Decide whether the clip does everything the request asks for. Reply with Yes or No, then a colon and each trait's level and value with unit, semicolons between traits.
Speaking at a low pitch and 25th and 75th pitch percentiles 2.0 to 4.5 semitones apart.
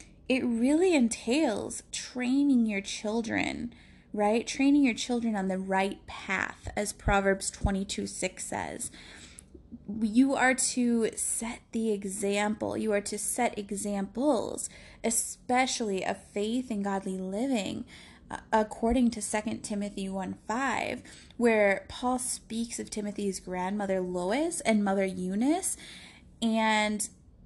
No: high, 220 Hz; average, 3.7 semitones